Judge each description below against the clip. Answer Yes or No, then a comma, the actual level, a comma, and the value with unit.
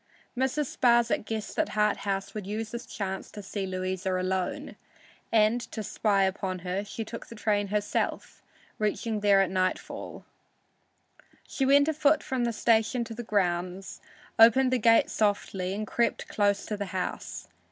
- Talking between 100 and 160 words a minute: Yes, average, 150 wpm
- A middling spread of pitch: Yes, average, 3.2 semitones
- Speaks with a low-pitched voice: No, high, 210 Hz